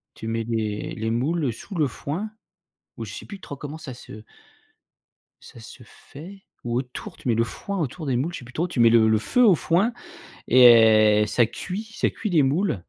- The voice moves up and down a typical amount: No, wide, 7.0 semitones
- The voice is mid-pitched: No, low, 125 Hz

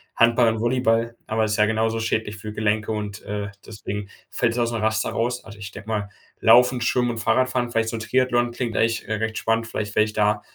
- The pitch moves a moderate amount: No, narrow, 1.7 semitones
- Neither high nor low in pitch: No, low, 110 Hz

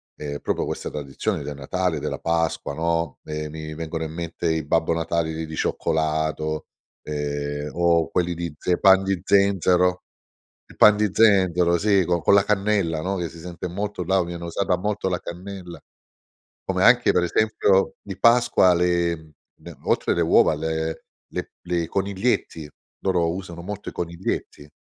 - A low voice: Yes, very low, 85 Hz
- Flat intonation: No, average, 3.0 semitones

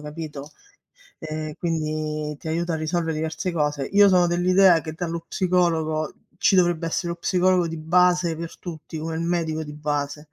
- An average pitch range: No, narrow, 2.1 semitones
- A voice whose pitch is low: No, medium, 165 Hz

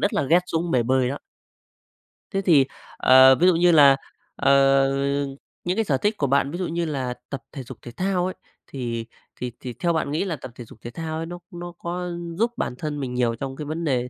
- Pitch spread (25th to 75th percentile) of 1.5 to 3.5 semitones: No, average, 5.1 semitones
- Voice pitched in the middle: Yes, medium, 145 Hz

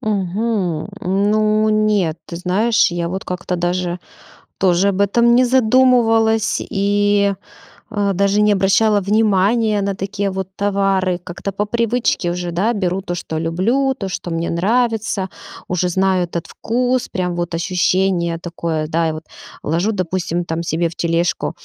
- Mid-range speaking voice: No, high, 195 Hz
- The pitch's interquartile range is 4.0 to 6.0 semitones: No, average, 3.5 semitones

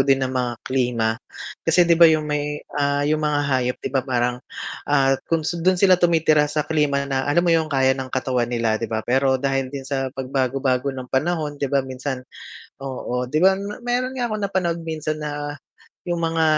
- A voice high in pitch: No, medium, 140 Hz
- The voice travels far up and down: No, average, 3.5 semitones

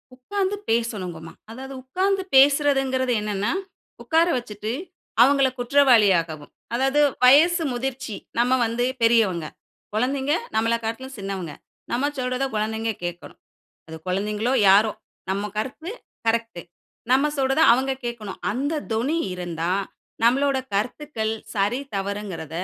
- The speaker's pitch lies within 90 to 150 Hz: No, high, 235 Hz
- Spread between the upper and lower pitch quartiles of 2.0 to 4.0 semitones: No, average, 4.5 semitones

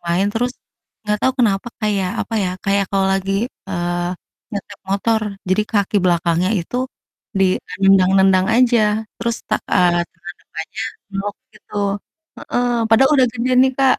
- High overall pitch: Yes, high, 200 Hz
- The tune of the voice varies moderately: Yes, average, 3.4 semitones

